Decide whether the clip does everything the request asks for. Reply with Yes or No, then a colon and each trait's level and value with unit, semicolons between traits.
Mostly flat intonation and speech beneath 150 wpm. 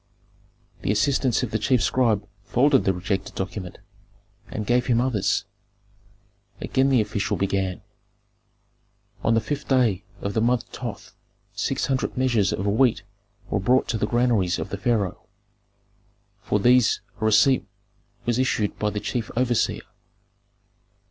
No: average, 3.8 semitones; average, 140 wpm